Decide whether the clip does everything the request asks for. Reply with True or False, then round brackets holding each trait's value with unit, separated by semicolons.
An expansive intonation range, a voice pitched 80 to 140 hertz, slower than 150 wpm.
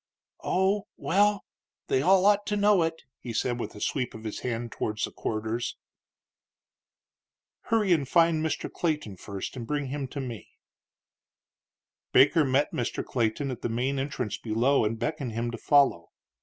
False (5.8 semitones; 135 Hz; 160 wpm)